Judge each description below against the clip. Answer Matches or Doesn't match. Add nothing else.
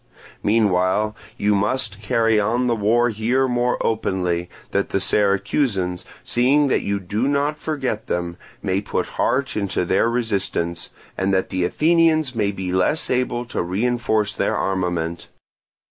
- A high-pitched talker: Doesn't match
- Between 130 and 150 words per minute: Matches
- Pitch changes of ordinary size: Matches